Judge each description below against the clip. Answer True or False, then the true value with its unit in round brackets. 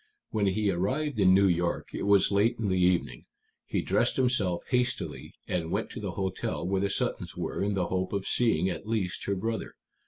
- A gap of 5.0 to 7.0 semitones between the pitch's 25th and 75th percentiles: False (2.8 semitones)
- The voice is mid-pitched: False (100 Hz)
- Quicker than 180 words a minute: True (200 wpm)